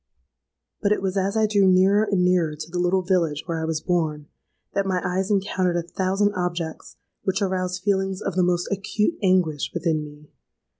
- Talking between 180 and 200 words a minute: Yes, average, 190 wpm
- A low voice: No, medium, 185 Hz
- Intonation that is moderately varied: No, narrow, 2.3 semitones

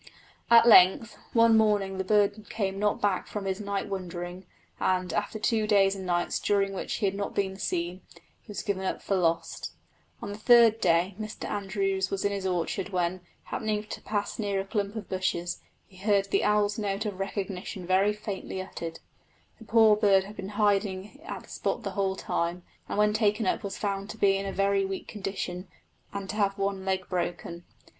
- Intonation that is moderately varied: No, narrow, 1.8 semitones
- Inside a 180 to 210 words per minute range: Yes, average, 200 wpm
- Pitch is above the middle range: Yes, high, 195 Hz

